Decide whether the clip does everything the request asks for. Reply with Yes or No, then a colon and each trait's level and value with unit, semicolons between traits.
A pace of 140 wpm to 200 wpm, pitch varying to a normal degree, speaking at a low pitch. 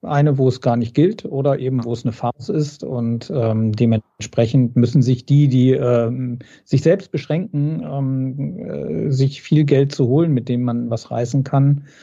Yes: average, 185 wpm; average, 3.0 semitones; low, 130 Hz